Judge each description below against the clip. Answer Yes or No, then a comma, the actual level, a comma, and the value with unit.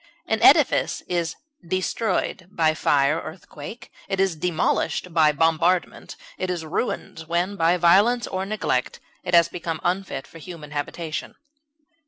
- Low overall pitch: No, medium, 170 Hz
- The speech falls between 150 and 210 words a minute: No, average, 140 wpm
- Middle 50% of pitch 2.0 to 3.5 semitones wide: Yes, average, 2.7 semitones